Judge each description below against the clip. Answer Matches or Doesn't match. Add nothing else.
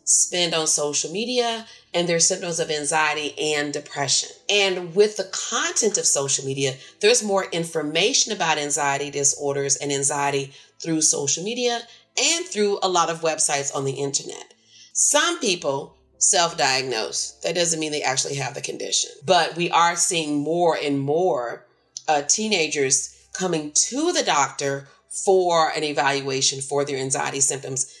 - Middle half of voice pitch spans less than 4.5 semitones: Doesn't match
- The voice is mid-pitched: Matches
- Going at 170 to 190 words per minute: Doesn't match